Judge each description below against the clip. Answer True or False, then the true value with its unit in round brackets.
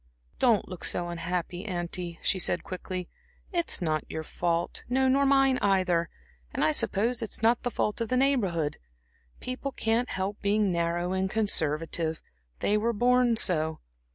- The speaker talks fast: False (155 wpm)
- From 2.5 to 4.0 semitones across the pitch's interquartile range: False (5.5 semitones)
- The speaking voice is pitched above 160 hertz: True (190 Hz)